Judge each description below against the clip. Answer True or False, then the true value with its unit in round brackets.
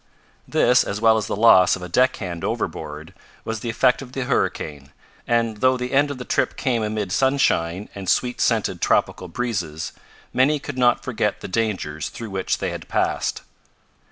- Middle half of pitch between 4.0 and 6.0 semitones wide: True (5.3 semitones)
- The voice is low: True (110 Hz)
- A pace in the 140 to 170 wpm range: False (180 wpm)